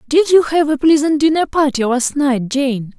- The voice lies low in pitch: No, very high, 285 Hz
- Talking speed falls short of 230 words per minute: Yes, average, 200 wpm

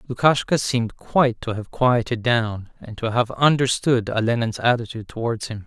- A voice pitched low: Yes, low, 120 Hz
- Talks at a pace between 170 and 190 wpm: No, average, 160 wpm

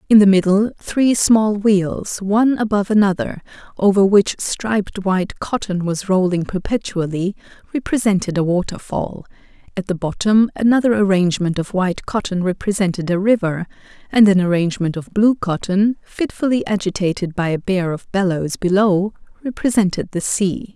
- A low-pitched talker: No, high, 195 Hz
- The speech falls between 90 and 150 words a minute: Yes, average, 140 wpm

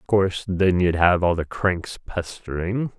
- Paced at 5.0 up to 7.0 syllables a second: No, 4.1 syllables/s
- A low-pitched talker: Yes, very low, 90 Hz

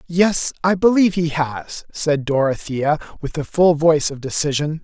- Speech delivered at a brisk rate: No, average, 160 wpm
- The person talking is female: No, male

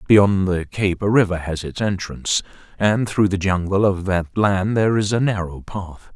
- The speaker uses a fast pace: No, average, 195 wpm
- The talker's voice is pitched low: Yes, very low, 95 Hz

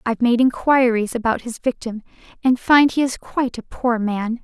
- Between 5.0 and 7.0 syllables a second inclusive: Yes, 5.1 syllables/s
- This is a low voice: No, high, 240 Hz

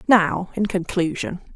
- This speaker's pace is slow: Yes, slow, 115 wpm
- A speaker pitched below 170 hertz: No, medium, 185 Hz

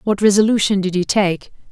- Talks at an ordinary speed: Yes, average, 175 wpm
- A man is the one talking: No, female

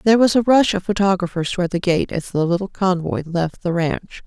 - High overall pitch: No, medium, 180 Hz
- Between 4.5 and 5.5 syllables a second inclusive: No, 5.9 syllables/s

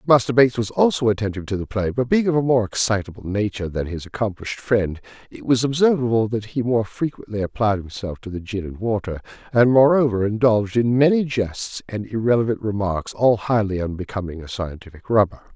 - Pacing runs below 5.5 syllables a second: No, 5.9 syllables/s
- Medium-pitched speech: No, low, 110 Hz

